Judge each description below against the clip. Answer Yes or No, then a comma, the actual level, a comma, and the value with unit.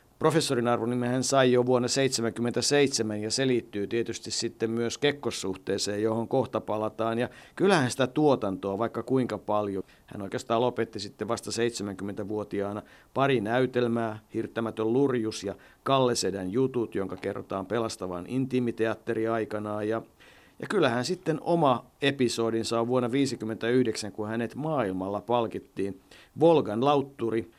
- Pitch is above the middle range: No, low, 115 Hz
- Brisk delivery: No, average, 125 wpm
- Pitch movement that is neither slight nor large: Yes, average, 3.0 semitones